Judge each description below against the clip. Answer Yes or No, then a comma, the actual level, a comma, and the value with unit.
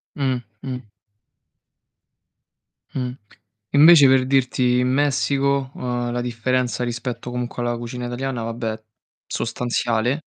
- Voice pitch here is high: No, low, 125 Hz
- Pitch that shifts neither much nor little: No, narrow, 1.8 semitones